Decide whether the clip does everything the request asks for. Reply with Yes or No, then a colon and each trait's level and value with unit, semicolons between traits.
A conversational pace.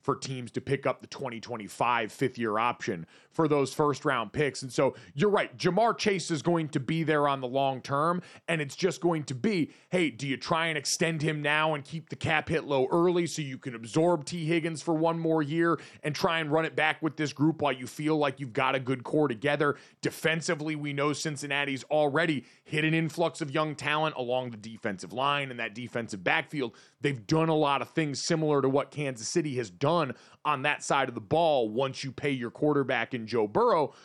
No: fast, 220 wpm